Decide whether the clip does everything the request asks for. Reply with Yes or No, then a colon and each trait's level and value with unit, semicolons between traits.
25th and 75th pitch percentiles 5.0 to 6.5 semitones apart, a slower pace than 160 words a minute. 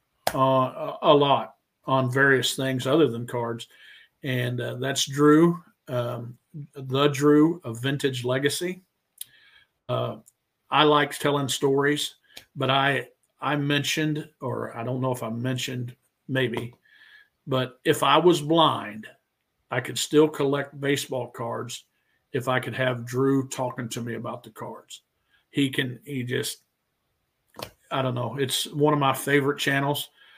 No: narrow, 2.6 semitones; average, 140 wpm